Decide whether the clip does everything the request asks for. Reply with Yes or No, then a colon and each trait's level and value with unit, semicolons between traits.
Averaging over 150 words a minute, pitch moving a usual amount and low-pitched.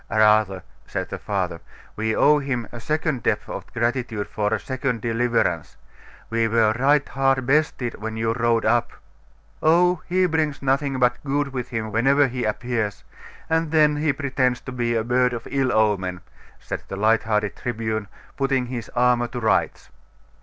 Yes: average, 165 wpm; average, 3.6 semitones; low, 120 Hz